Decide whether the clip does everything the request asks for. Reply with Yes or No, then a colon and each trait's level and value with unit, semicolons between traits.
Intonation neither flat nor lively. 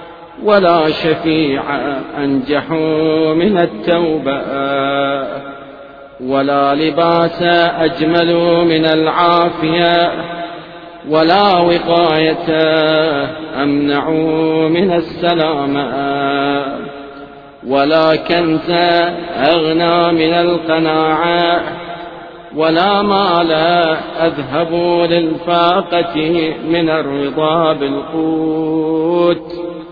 No: narrow, 1.6 semitones